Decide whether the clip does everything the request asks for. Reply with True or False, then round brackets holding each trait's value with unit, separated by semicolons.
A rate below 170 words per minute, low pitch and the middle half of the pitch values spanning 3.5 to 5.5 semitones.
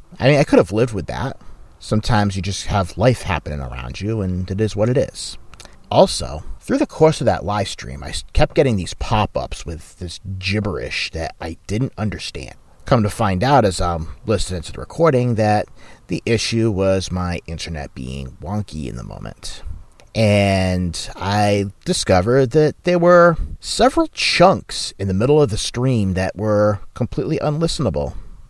False (175 wpm; 100 Hz; 4.8 semitones)